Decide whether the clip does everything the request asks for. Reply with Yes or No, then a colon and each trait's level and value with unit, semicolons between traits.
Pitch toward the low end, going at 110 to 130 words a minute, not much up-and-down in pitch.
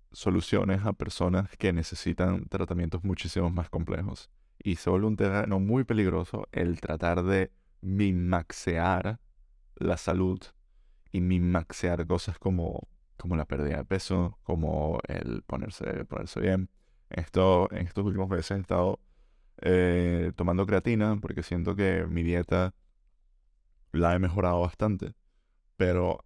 Yes: very low, 90 Hz; slow, 125 wpm; narrow, 2.1 semitones